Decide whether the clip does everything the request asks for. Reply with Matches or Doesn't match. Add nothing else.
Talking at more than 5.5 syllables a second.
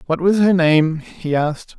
Doesn't match